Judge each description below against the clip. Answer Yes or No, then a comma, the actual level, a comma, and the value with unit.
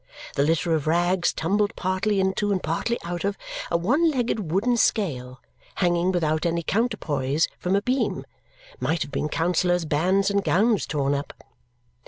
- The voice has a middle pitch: Yes, medium, 180 Hz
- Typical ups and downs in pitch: Yes, average, 4.0 semitones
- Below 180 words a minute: Yes, average, 160 wpm